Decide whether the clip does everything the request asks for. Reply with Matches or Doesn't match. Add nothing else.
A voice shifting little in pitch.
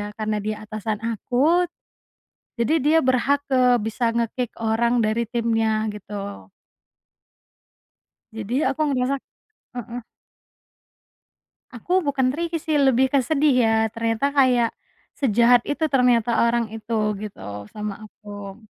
Doesn't match